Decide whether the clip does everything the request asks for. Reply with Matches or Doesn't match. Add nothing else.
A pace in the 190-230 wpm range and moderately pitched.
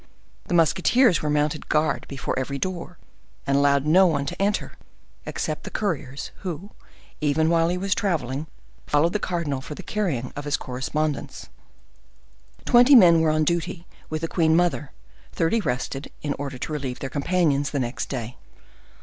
Doesn't match